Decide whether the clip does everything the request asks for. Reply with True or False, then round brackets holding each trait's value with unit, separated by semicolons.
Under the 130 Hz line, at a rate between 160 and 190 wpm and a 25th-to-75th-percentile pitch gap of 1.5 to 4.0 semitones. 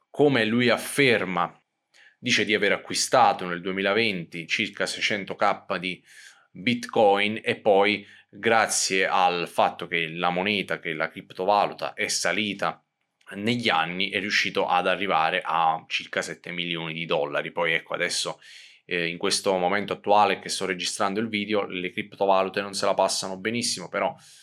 False (100 Hz; 145 wpm; 2.8 semitones)